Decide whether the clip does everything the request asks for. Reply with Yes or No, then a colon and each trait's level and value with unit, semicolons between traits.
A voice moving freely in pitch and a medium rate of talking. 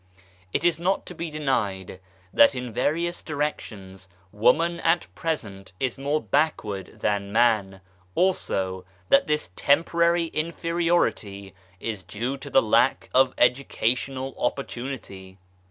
No: wide, 7.7 semitones; slow, 120 wpm